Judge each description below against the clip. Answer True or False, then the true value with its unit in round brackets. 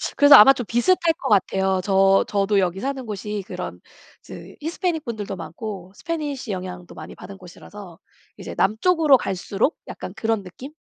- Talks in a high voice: True (210 Hz)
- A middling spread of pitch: False (6.1 semitones)